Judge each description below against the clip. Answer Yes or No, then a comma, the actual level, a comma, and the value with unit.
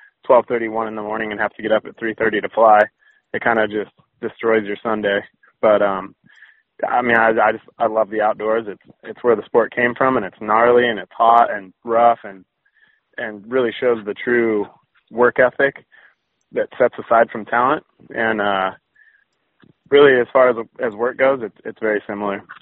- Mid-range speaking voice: No, low, 110 Hz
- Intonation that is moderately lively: No, narrow, 2.3 semitones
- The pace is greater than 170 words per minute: Yes, average, 200 wpm